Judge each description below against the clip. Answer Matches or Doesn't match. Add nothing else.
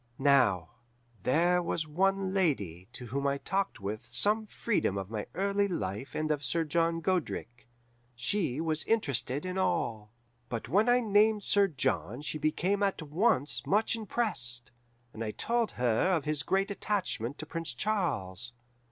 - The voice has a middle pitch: Matches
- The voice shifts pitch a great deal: Matches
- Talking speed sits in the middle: Matches